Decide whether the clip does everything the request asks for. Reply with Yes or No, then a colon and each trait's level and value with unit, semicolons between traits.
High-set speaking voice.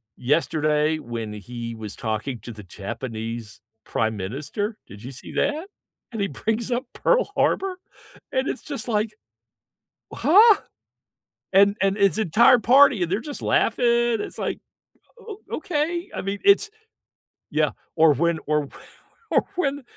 Yes: high, 195 Hz